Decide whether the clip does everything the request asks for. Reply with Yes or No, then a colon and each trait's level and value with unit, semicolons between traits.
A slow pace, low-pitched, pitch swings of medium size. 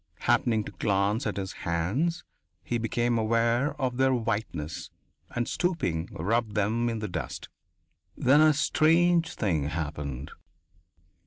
No: slow, 130 wpm; low, 115 Hz; wide, 6.6 semitones